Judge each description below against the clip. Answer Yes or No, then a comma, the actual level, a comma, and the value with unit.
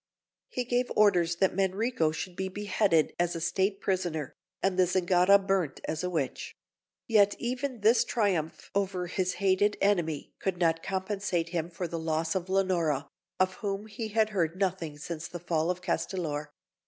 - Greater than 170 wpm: No, average, 165 wpm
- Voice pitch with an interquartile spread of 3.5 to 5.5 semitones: No, average, 3.1 semitones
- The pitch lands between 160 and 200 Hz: Yes, medium, 185 Hz